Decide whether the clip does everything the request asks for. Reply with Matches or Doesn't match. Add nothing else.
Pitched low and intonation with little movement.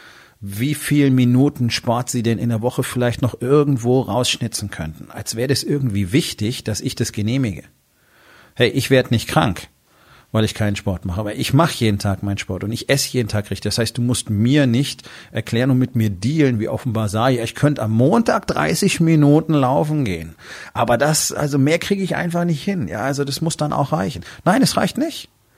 Doesn't match